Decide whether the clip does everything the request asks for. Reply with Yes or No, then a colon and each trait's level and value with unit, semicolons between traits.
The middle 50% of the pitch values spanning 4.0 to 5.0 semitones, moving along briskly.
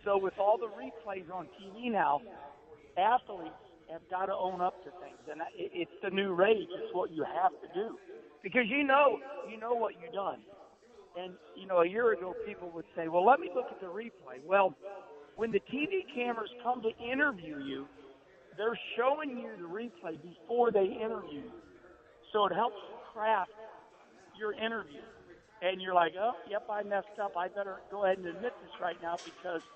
No: average, 4.7 semitones; average, 190 wpm